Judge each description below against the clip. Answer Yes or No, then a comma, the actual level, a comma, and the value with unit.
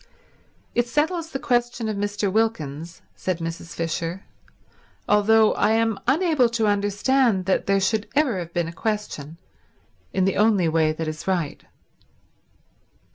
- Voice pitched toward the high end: Yes, high, 205 Hz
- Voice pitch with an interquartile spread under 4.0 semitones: No, average, 5.1 semitones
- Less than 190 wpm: Yes, average, 140 wpm